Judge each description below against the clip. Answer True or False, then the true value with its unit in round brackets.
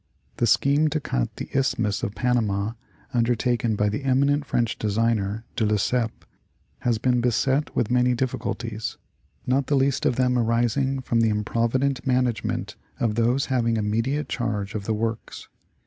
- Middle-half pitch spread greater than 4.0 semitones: False (3.0 semitones)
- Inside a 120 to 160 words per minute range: True (155 wpm)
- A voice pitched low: True (120 Hz)